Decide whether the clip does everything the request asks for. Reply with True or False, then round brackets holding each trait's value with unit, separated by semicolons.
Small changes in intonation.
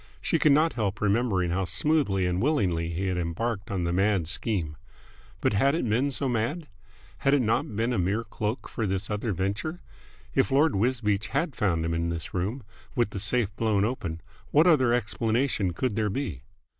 False (5.1 semitones)